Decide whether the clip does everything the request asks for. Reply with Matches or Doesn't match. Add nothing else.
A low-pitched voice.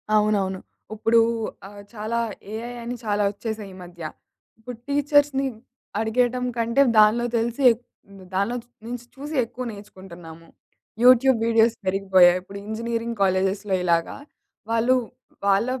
Doesn't match